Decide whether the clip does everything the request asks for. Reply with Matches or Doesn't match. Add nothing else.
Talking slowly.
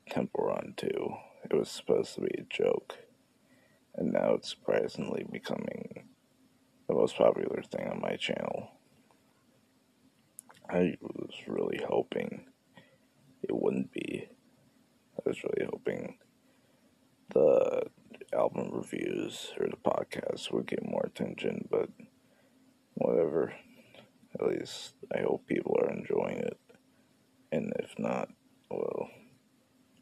Matches